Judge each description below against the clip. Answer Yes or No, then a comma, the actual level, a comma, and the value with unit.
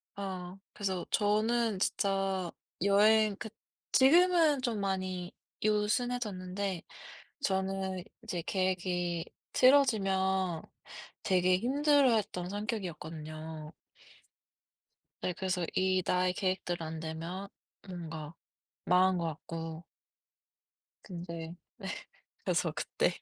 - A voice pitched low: No, high, 190 Hz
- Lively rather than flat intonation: No, average, 3.1 semitones